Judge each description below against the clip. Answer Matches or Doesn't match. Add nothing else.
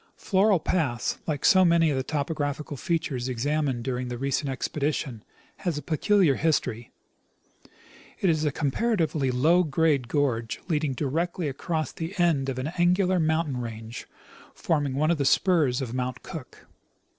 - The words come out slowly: Doesn't match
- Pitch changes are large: Doesn't match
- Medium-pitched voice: Matches